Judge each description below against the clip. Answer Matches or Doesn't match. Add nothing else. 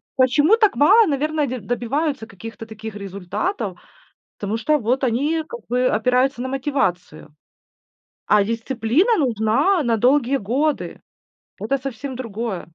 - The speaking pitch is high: Matches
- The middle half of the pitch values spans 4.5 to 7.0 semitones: Matches